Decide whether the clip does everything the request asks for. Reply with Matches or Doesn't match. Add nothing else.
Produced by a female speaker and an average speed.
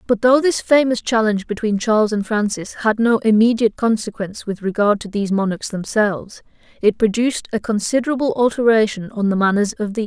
Matches